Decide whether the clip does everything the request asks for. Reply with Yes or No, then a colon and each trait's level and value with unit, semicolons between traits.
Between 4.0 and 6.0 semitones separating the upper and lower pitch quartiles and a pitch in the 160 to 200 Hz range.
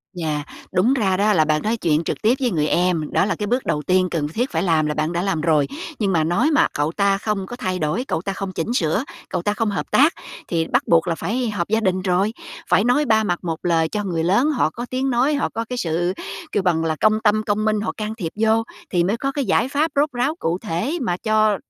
Yes: average, 5.2 semitones; high, 195 Hz